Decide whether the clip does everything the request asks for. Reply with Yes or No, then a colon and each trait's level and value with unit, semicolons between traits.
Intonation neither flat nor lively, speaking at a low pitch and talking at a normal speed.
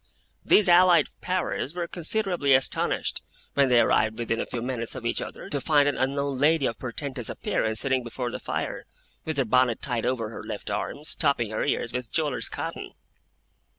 Yes: average, 4.2 semitones; low, 130 Hz; average, 185 wpm